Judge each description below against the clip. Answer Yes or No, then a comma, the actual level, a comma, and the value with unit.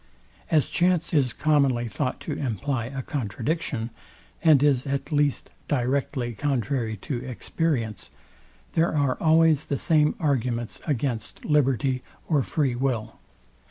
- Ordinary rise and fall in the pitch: Yes, average, 3.7 semitones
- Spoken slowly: Yes, slow, 125 wpm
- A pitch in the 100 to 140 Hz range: Yes, low, 135 Hz